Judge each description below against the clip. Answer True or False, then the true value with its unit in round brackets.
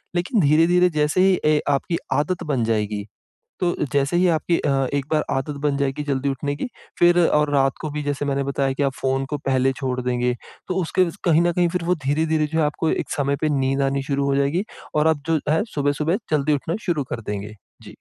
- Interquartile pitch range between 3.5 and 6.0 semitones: False (2.9 semitones)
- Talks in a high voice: False (145 Hz)